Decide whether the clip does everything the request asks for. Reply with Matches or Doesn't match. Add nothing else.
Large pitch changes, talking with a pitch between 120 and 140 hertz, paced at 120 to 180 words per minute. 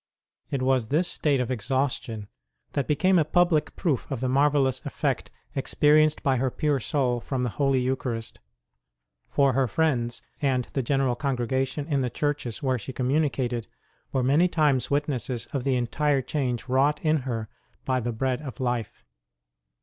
Doesn't match